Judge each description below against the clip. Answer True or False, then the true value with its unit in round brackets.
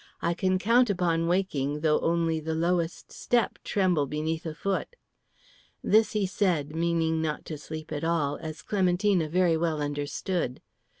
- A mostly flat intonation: False (3.0 semitones)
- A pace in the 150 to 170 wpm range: True (155 wpm)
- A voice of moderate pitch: True (165 Hz)